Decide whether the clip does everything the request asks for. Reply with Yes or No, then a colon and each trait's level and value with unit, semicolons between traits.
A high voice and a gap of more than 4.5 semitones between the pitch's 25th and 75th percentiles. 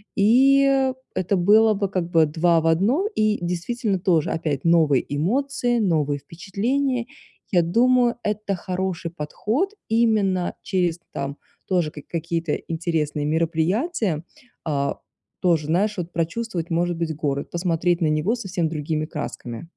No: medium, 175 Hz; average, 4.9 semitones